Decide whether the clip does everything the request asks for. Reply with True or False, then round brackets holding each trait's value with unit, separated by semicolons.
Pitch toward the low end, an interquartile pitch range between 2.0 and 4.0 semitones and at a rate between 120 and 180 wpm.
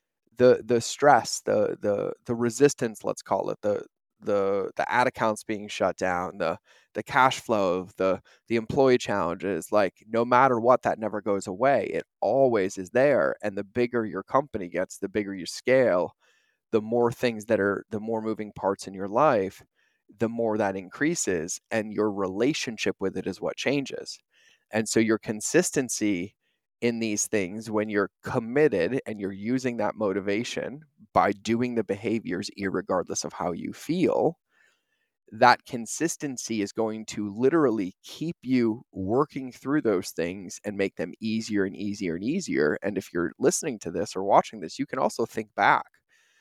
True (110 Hz; 3.7 semitones; 170 wpm)